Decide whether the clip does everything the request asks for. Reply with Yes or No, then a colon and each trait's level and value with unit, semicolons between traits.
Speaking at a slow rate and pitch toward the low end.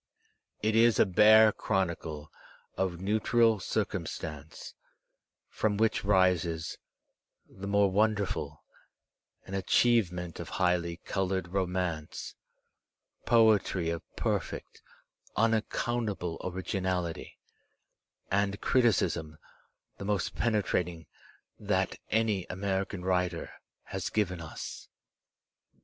Yes: slow, 95 wpm; very low, 95 Hz